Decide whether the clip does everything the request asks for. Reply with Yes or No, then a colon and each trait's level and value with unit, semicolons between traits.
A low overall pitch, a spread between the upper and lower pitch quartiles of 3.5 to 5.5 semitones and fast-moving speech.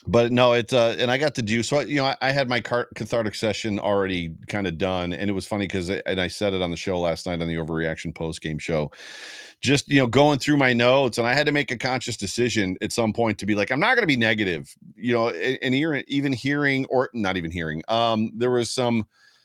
Yes: low, 115 Hz; average, 5.2 semitones; fast, 260 wpm